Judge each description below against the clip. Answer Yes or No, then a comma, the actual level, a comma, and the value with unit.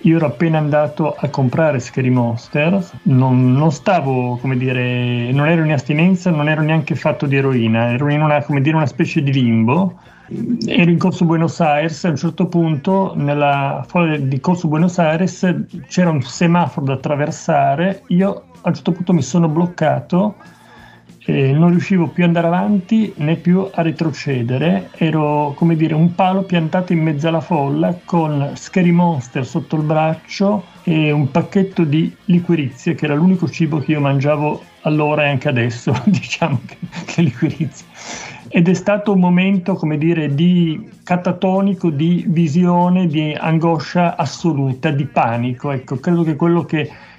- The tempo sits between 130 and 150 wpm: No, average, 165 wpm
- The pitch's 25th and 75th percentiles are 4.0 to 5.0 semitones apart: No, average, 3.2 semitones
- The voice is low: No, medium, 160 Hz